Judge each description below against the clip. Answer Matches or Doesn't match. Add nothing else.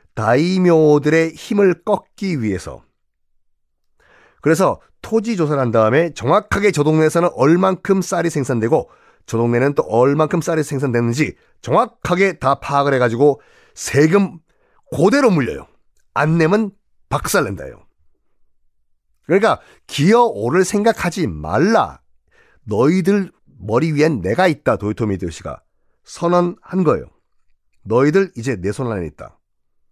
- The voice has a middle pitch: Matches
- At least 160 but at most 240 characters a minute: Doesn't match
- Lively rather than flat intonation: Matches